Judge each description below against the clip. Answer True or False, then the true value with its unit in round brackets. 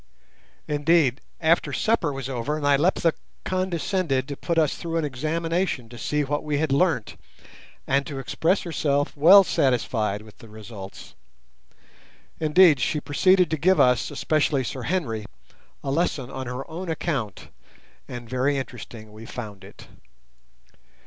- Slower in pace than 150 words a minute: True (140 wpm)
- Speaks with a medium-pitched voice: True (145 Hz)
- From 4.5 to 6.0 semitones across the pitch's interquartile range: True (4.8 semitones)